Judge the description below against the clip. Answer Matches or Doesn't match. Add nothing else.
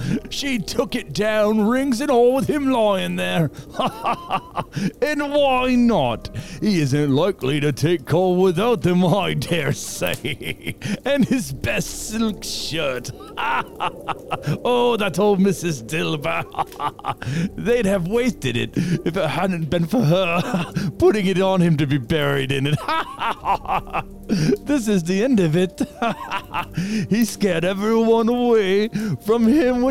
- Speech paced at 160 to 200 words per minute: Doesn't match